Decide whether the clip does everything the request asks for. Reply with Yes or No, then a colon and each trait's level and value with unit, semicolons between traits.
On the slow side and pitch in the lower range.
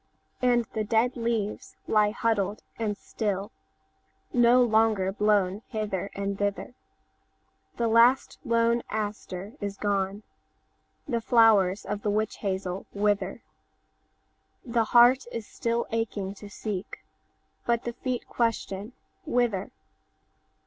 No: slow, 100 wpm; high, 215 Hz